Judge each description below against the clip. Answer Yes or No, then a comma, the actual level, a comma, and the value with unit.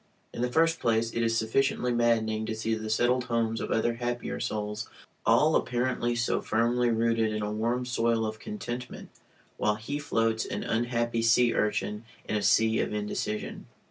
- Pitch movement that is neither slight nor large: No, narrow, 1.7 semitones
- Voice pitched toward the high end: No, low, 115 Hz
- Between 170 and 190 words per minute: Yes, average, 175 wpm